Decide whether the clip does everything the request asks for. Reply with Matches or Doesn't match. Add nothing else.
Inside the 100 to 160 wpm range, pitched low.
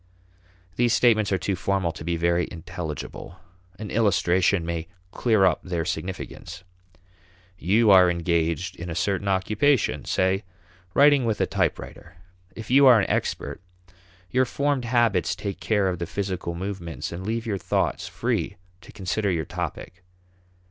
Matches